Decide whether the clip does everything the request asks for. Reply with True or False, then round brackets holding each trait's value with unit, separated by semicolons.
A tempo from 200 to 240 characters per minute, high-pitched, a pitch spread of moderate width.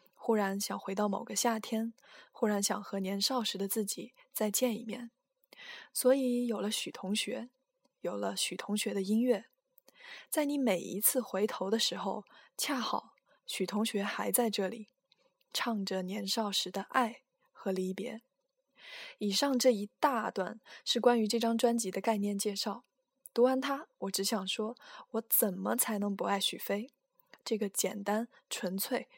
True (220 characters per minute; 225 Hz; 4.1 semitones)